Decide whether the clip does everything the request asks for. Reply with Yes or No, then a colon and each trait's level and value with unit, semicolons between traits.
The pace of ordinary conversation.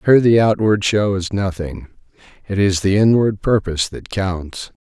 Yes: average, 160 wpm